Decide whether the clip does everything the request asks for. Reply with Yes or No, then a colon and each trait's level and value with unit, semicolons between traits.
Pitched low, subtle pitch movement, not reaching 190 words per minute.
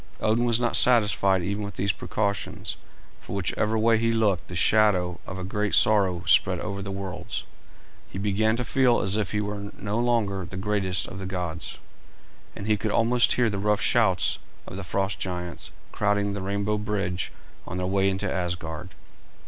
Yes: low, 100 Hz; narrow, 2.3 semitones; average, 180 wpm